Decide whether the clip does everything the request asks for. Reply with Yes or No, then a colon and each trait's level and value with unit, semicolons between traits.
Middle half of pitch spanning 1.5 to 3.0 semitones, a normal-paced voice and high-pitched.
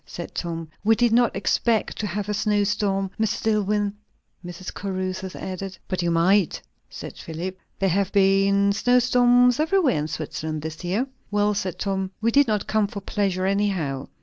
Yes: narrow, 2.4 semitones; average, 175 wpm; high, 200 Hz